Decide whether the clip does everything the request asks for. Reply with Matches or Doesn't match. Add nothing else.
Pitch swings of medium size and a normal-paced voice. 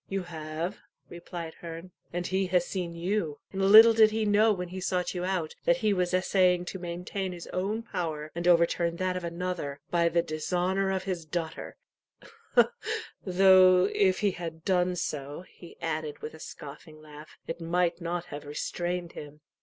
Doesn't match